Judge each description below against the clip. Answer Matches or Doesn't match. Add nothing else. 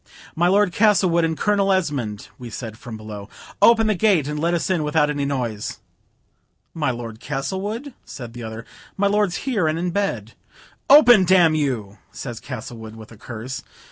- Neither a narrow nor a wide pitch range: Doesn't match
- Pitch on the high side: Doesn't match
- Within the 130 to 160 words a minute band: Doesn't match